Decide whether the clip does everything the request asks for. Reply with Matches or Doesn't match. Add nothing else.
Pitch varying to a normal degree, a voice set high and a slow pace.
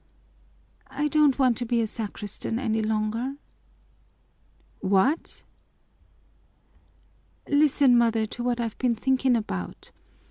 Matches